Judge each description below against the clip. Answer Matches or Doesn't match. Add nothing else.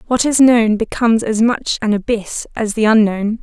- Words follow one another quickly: Doesn't match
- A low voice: Doesn't match